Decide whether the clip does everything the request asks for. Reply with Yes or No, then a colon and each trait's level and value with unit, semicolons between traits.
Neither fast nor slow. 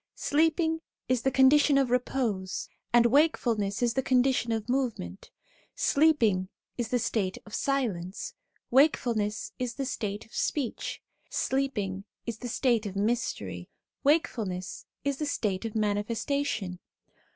No: slow, 130 wpm